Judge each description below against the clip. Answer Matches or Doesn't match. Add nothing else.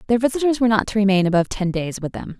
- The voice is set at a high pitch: Matches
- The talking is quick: Matches